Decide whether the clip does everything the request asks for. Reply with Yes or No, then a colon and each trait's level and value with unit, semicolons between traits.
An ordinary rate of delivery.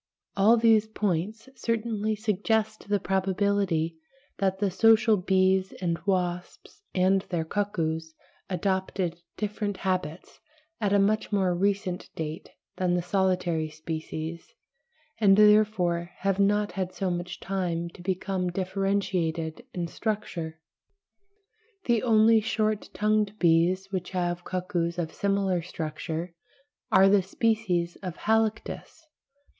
No: slow, 120 wpm